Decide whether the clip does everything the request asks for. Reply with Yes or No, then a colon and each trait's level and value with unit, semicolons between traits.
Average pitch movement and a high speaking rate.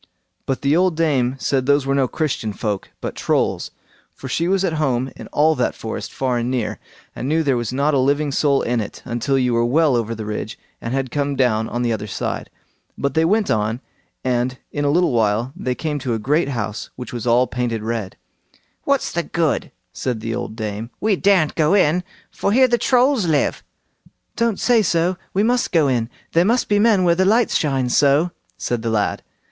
No: wide, 5.8 semitones; fast, 210 wpm